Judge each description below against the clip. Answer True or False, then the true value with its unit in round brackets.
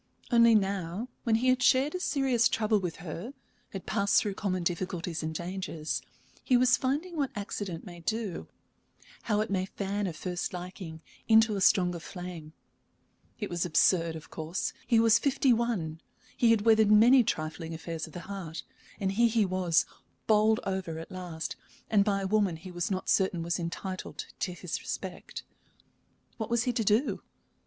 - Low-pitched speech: False (195 Hz)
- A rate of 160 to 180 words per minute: True (175 wpm)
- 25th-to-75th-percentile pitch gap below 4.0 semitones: False (4.5 semitones)